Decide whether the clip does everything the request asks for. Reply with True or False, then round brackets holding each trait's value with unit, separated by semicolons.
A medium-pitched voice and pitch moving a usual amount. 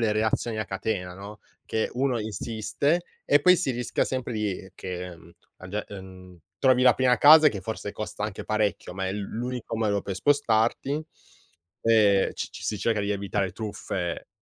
False (110 Hz; 3.7 semitones)